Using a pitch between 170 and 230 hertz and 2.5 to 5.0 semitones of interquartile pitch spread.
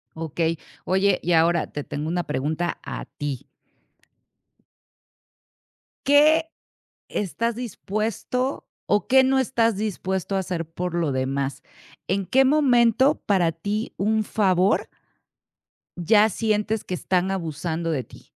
No: high, 190 Hz; wide, 5.4 semitones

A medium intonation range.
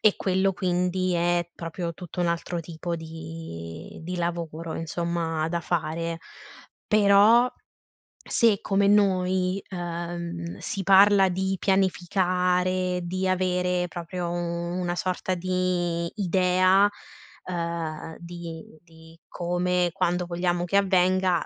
No: narrow, 1.6 semitones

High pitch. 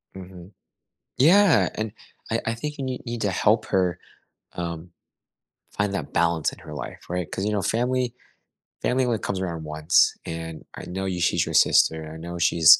No: very low, 95 Hz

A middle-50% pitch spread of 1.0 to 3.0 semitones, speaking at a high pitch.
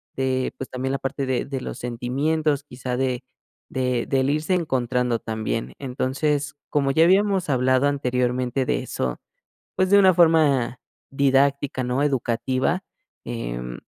No: narrow, 2.6 semitones; low, 130 Hz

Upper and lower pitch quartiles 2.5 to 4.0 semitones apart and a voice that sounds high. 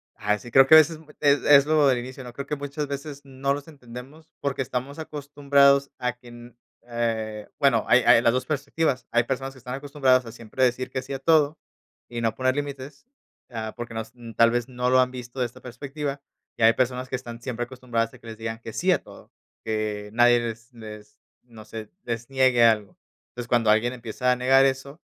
No: average, 3.0 semitones; low, 125 Hz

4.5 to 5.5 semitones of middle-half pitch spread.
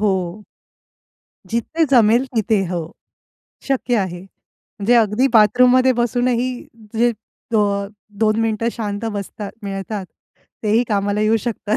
No: average, 2.9 semitones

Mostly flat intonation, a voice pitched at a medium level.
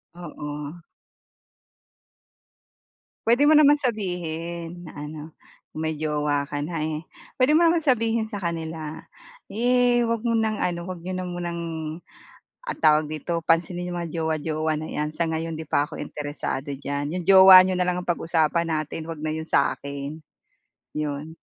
No: average, 3.3 semitones; medium, 165 Hz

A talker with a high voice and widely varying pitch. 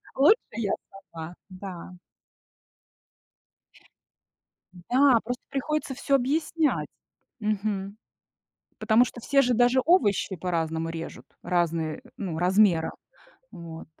Yes: high, 205 Hz; wide, 6.9 semitones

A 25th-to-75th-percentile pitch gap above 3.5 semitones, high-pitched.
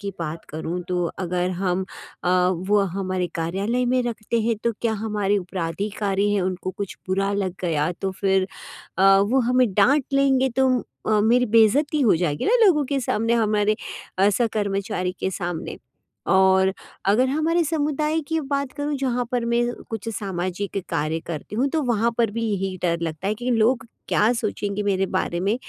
Yes: average, 4.5 semitones; high, 205 Hz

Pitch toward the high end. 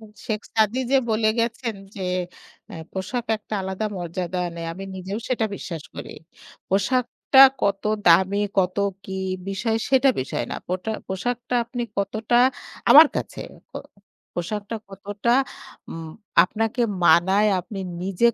Yes: high, 205 Hz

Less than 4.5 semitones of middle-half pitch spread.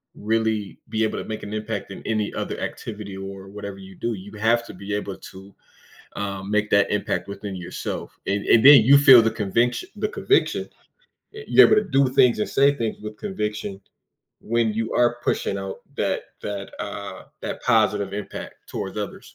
Yes: average, 2.8 semitones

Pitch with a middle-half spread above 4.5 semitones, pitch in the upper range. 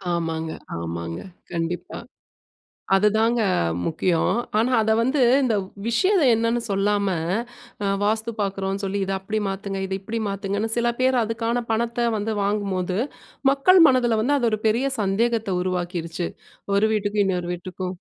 No: average, 3.7 semitones; high, 205 Hz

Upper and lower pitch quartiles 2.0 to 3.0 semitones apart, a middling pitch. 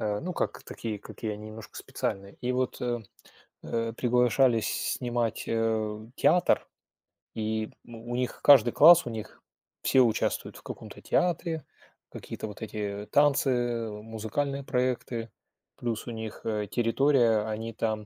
No: narrow, 2.6 semitones; low, 115 Hz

